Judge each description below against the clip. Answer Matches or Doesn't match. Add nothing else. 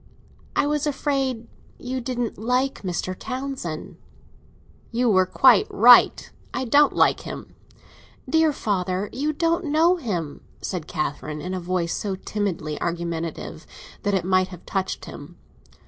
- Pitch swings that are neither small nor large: Doesn't match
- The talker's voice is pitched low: Doesn't match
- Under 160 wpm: Matches